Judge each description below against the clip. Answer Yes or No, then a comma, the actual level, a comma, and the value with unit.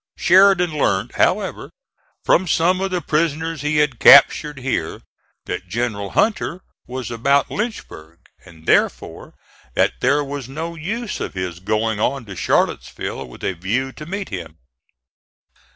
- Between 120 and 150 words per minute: Yes, average, 140 wpm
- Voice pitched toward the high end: No, medium, 140 Hz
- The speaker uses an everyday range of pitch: No, wide, 7.8 semitones